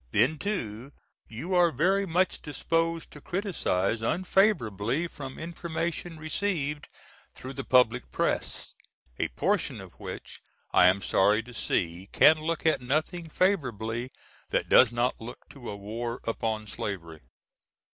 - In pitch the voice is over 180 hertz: No, low, 135 Hz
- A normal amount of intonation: No, wide, 6.9 semitones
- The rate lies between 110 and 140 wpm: Yes, slow, 135 wpm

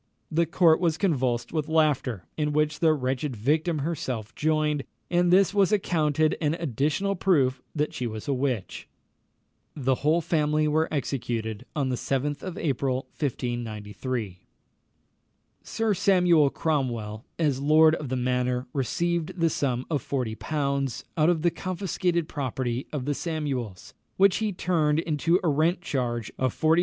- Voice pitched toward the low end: No, medium, 150 Hz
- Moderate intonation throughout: Yes, average, 4.4 semitones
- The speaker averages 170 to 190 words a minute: No, average, 150 wpm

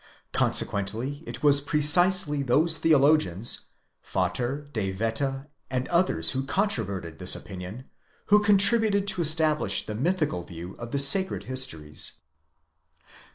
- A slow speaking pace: Yes, slow, 115 wpm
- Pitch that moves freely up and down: Yes, wide, 7.3 semitones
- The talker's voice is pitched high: No, medium, 140 Hz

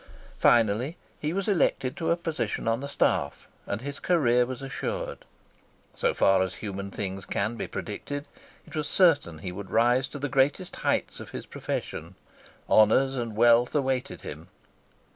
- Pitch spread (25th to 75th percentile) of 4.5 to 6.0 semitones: Yes, wide, 5.5 semitones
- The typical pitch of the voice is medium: No, low, 125 Hz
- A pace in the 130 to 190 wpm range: Yes, average, 165 wpm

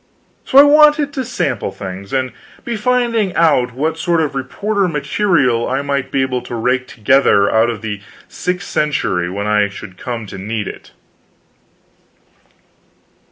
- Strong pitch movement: Yes, wide, 8.4 semitones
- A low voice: Yes, low, 130 Hz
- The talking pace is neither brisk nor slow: Yes, average, 155 wpm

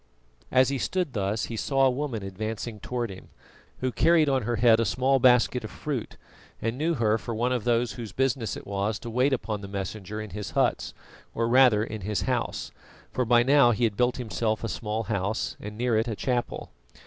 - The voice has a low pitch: Yes, low, 115 Hz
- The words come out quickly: Yes, fast, 210 wpm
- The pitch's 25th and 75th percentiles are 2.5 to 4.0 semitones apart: Yes, average, 3.0 semitones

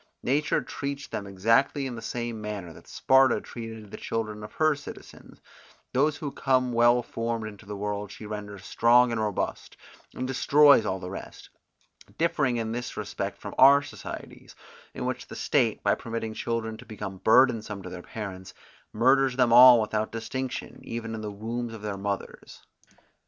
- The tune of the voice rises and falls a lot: No, average, 3.3 semitones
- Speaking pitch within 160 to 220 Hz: No, low, 115 Hz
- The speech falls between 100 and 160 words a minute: No, average, 170 wpm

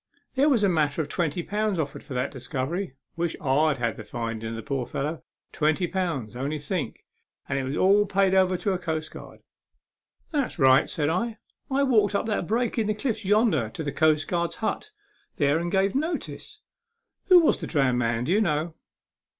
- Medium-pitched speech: Yes, medium, 165 Hz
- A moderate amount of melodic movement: No, wide, 6.6 semitones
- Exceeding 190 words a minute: Yes, average, 200 wpm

